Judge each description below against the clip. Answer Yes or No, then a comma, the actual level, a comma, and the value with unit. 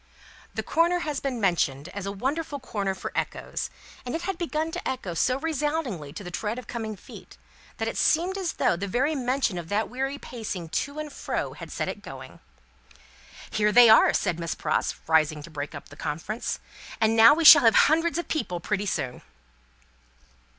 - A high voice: Yes, high, 225 Hz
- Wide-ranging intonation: Yes, wide, 8.4 semitones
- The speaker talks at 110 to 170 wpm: No, average, 190 wpm